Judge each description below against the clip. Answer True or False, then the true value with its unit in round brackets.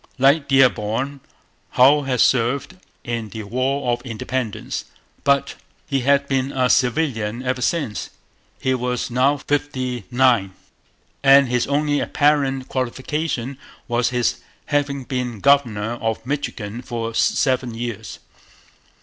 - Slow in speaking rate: True (120 wpm)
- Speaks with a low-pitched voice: True (130 Hz)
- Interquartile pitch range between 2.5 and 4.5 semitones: True (2.8 semitones)